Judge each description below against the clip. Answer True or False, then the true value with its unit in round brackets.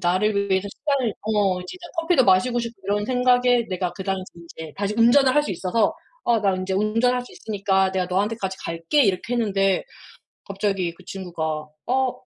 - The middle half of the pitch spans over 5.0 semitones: False (4.3 semitones)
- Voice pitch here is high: True (200 Hz)